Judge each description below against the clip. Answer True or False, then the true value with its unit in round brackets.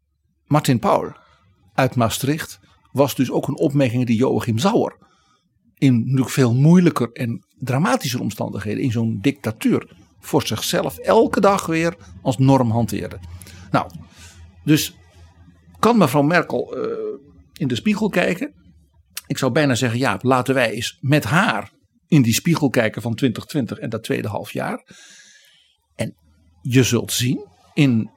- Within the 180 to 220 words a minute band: False (140 wpm)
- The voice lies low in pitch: True (130 Hz)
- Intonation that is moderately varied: False (6.9 semitones)